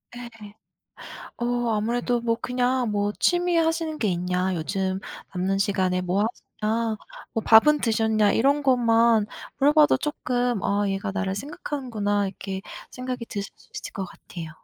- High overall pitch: Yes, high, 225 Hz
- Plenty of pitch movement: No, average, 4.0 semitones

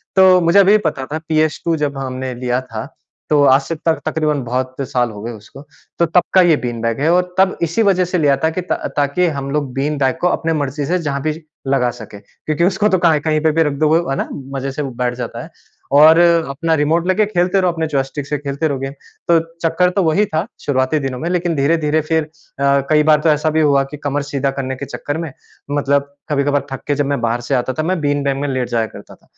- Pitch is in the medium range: Yes, medium, 150 Hz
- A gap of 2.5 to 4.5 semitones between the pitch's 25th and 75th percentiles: Yes, average, 3.4 semitones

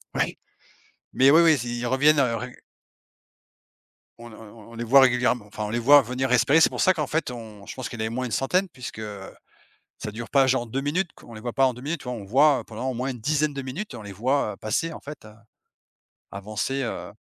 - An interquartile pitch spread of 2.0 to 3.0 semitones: No, average, 3.4 semitones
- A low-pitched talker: Yes, low, 125 Hz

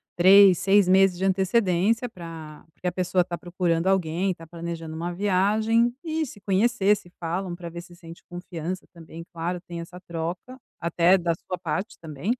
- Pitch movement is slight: Yes, narrow, 2.3 semitones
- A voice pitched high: No, medium, 180 Hz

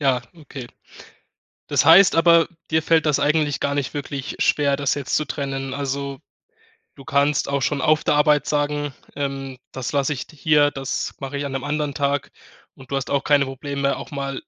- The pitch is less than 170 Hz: Yes, medium, 140 Hz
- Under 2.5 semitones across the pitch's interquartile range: Yes, narrow, 1.3 semitones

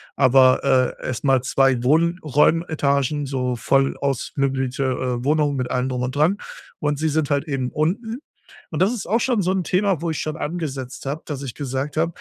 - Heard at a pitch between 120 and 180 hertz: Yes, medium, 140 Hz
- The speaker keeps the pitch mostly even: No, average, 3.4 semitones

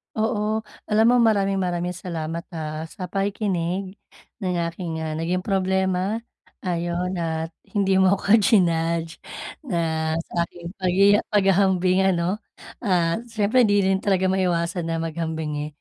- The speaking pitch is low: No, medium, 185 Hz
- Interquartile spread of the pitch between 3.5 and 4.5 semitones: No, average, 2.9 semitones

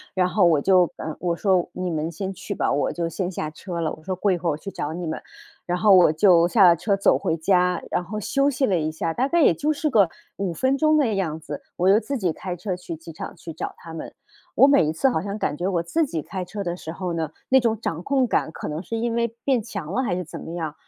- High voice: No, medium, 180 Hz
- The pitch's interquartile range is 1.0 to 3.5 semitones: No, average, 4.4 semitones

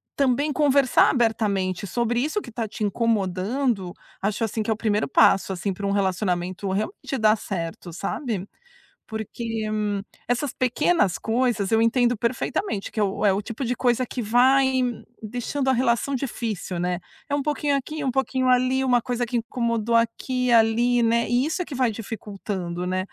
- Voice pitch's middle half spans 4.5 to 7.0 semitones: No, average, 3.8 semitones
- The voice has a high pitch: Yes, high, 230 Hz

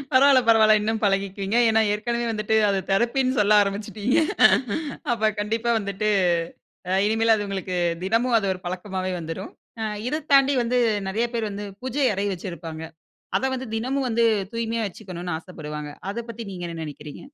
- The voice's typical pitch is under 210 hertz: No, high, 215 Hz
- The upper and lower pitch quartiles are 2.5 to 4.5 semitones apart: Yes, average, 3.7 semitones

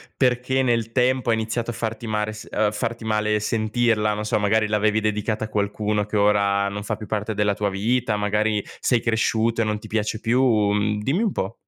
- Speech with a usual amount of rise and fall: No, narrow, 1.8 semitones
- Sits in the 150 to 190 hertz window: No, low, 110 Hz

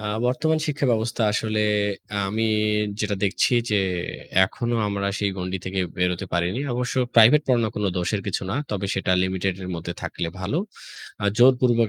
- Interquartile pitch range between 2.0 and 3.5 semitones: No, average, 4.2 semitones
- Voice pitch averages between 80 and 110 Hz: Yes, low, 105 Hz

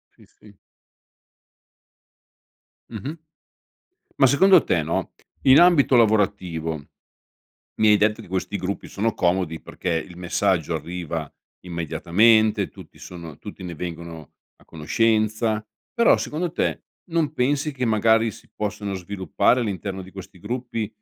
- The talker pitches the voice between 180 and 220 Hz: No, low, 105 Hz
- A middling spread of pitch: Yes, average, 4.8 semitones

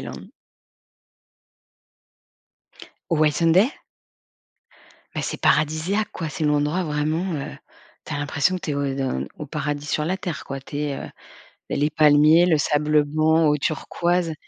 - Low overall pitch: No, medium, 150 Hz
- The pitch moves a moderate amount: No, narrow, 2.0 semitones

